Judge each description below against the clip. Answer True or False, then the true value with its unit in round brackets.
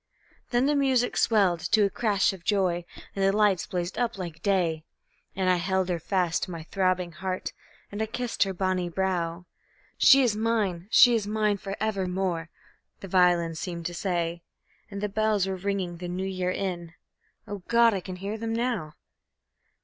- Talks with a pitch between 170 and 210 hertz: True (190 Hz)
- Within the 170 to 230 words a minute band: True (180 wpm)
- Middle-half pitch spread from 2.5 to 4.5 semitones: True (3.0 semitones)